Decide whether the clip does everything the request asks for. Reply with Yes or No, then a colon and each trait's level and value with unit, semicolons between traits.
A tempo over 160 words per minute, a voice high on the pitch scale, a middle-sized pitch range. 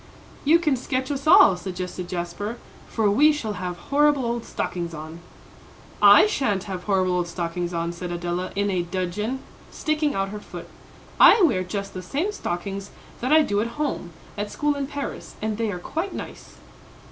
No: average, 180 wpm; high, 205 Hz; wide, 7.5 semitones